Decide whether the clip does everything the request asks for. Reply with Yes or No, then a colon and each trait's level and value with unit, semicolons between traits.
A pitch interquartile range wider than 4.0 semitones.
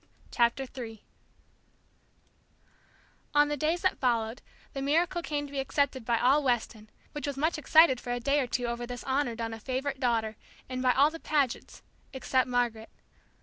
No: average, 3.3 semitones